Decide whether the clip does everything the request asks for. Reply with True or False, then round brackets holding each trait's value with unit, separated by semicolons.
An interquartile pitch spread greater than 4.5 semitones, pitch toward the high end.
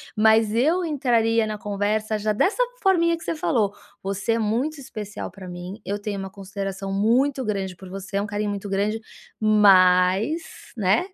False (2.9 semitones; 210 Hz)